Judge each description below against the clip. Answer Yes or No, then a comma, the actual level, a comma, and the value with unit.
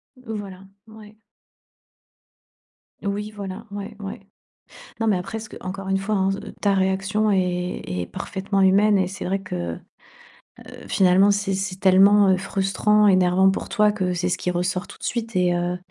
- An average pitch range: No, narrow, 1.9 semitones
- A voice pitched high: Yes, high, 195 Hz